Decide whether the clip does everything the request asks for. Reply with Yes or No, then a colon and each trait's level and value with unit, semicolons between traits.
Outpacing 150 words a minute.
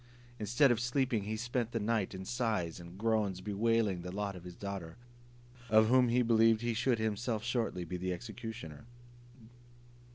Yes: average, 165 wpm